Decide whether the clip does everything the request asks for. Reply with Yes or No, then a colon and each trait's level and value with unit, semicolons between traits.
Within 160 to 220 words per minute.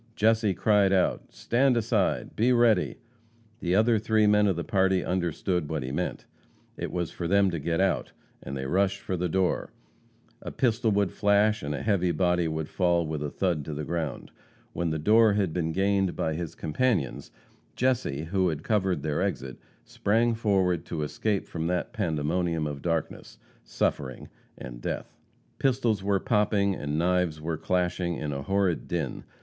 Yes: average, 175 wpm